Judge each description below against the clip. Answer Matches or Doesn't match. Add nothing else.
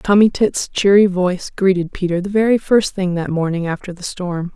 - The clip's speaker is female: Matches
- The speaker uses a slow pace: Doesn't match